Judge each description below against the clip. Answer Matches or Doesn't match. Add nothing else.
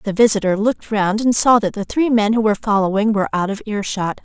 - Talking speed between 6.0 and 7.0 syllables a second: Matches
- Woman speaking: Matches